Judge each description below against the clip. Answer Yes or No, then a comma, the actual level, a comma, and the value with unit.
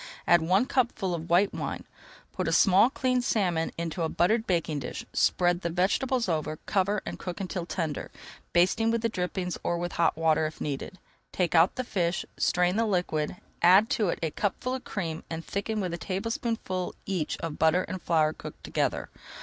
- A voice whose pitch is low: No, medium, 180 Hz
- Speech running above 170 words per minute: Yes, average, 190 wpm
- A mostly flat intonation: No, average, 3.6 semitones